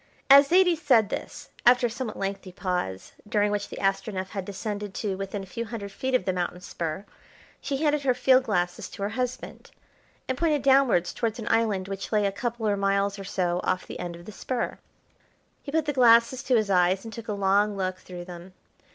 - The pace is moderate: No, fast, 210 wpm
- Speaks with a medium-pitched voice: No, high, 205 Hz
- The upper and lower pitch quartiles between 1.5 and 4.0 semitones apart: No, average, 4.5 semitones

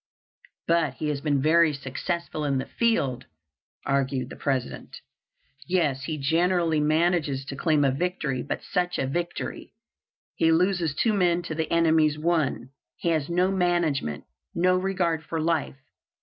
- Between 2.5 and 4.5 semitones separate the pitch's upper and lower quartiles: Yes, average, 3.7 semitones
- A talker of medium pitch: Yes, medium, 160 Hz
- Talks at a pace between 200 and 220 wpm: No, average, 150 wpm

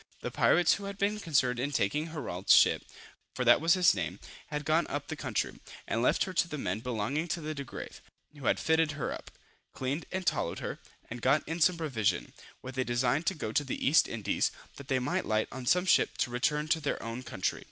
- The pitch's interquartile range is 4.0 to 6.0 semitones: Yes, average, 4.8 semitones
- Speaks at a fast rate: Yes, fast, 225 wpm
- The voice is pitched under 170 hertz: Yes, medium, 140 Hz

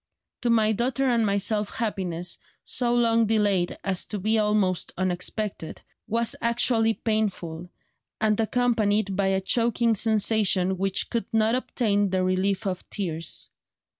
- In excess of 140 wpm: No, slow, 135 wpm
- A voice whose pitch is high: Yes, high, 210 Hz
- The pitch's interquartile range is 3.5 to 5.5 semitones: No, average, 3.1 semitones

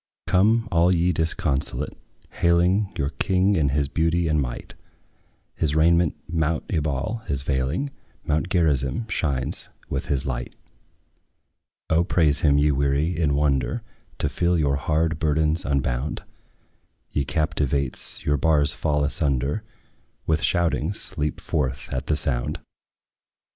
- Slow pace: Yes, slow, 125 wpm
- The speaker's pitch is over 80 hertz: No, very low, 75 Hz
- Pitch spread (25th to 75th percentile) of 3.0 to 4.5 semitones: Yes, average, 3.4 semitones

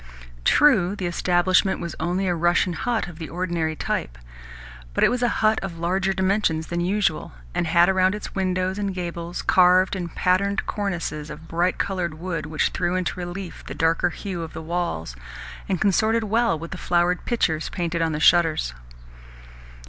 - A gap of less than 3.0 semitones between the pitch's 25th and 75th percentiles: Yes, narrow, 2.4 semitones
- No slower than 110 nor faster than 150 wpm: No, average, 175 wpm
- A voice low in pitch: No, medium, 175 Hz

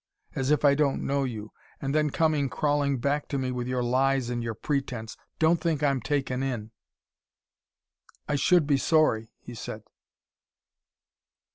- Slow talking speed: No, average, 155 wpm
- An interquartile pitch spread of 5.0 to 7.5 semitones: No, average, 3.1 semitones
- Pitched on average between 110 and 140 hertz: Yes, low, 135 Hz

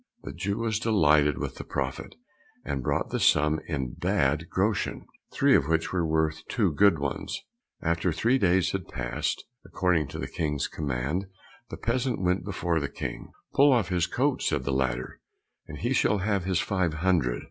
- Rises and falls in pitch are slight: No, average, 5.0 semitones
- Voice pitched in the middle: No, very low, 85 Hz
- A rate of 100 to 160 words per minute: No, average, 180 wpm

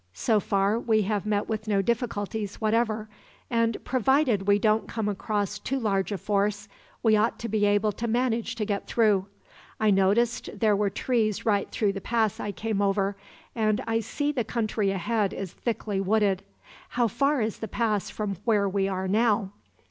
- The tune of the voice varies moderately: No, narrow, 2.2 semitones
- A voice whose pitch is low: No, high, 215 Hz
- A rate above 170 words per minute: Yes, average, 180 wpm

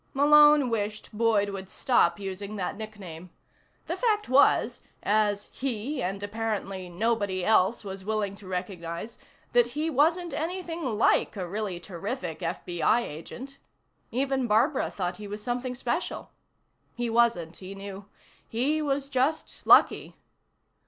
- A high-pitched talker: Yes, high, 215 Hz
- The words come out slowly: Yes, slow, 130 wpm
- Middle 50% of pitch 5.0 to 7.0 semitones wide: Yes, average, 5.3 semitones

